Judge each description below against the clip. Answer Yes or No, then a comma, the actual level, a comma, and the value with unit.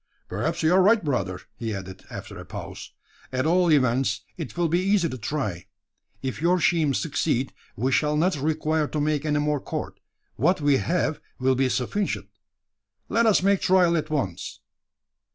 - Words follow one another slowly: No, average, 170 wpm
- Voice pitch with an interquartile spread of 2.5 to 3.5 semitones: No, average, 4.8 semitones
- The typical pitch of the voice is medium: Yes, medium, 150 Hz